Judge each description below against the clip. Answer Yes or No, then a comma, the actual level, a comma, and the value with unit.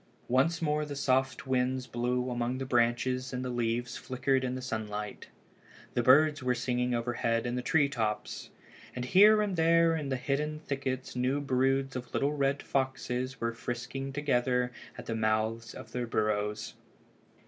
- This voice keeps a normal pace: Yes, average, 165 wpm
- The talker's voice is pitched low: Yes, low, 130 Hz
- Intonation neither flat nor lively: No, narrow, 2.3 semitones